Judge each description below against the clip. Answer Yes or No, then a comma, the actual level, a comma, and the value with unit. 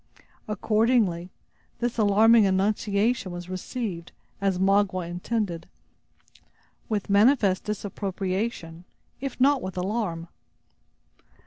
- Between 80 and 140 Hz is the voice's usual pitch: No, high, 200 Hz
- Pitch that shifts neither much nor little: Yes, average, 3.5 semitones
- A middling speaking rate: No, slow, 85 wpm